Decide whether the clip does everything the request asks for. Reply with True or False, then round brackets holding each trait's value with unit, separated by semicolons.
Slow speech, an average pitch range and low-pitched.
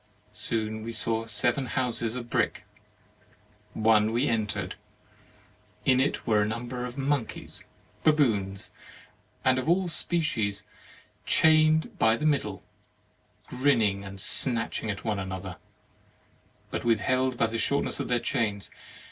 True (130 wpm; 3.5 semitones; 115 Hz)